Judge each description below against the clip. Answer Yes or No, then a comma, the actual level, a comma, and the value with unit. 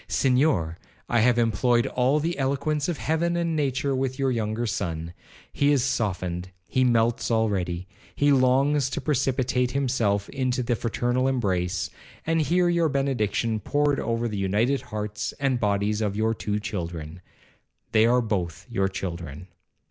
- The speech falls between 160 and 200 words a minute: No, average, 140 wpm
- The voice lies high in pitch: No, low, 120 Hz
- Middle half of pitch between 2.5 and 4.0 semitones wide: No, average, 5.1 semitones